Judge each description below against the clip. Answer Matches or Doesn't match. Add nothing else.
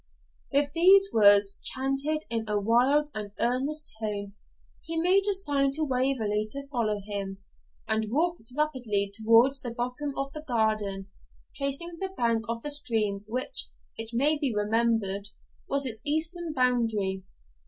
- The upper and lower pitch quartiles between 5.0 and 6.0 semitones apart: Matches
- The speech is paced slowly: Doesn't match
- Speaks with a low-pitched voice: Doesn't match